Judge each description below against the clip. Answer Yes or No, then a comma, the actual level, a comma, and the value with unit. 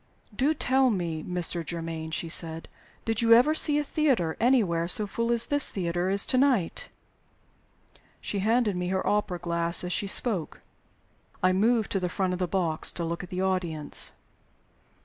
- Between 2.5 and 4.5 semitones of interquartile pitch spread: No, wide, 5.4 semitones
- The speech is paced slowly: No, average, 175 wpm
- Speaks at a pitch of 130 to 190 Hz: Yes, medium, 185 Hz